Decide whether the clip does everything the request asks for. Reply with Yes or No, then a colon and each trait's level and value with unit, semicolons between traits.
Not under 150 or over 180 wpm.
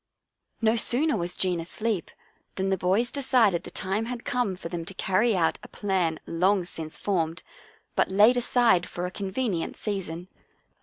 Yes: average, 170 wpm